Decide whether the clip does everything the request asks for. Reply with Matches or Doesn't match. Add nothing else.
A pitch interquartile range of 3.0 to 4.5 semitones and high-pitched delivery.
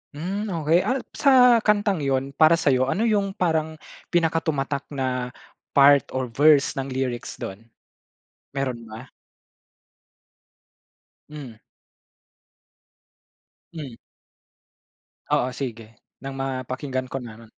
Doesn't match